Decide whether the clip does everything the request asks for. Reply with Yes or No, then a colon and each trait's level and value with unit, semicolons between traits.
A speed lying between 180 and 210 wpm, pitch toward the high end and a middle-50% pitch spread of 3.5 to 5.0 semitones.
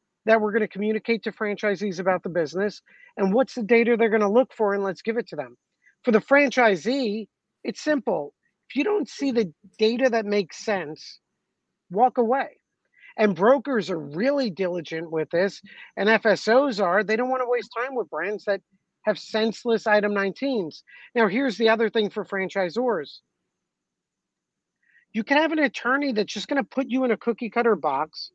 Yes: average, 185 wpm; high, 220 Hz; average, 3.9 semitones